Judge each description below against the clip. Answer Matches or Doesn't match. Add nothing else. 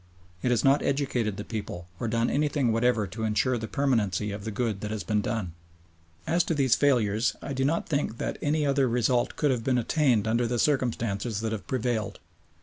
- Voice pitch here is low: Matches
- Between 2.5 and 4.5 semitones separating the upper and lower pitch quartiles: Matches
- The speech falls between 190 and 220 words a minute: Matches